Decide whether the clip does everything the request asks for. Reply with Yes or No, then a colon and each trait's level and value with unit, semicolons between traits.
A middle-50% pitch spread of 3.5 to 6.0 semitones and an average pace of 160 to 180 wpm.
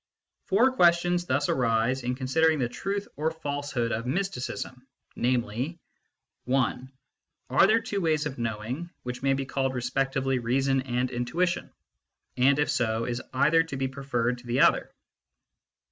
No: average, 4.2 semitones; average, 145 wpm